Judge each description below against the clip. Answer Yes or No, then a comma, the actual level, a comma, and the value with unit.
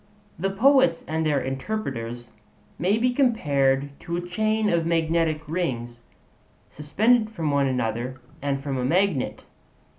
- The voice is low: No, medium, 160 Hz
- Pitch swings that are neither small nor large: No, wide, 6.8 semitones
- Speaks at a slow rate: Yes, slow, 130 wpm